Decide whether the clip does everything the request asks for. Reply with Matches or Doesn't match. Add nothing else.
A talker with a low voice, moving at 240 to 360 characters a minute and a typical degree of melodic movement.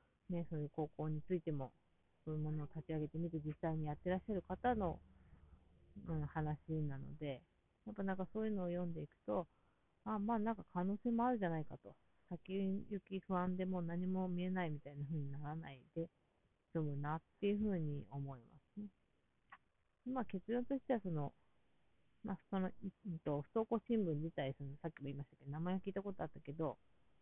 Doesn't match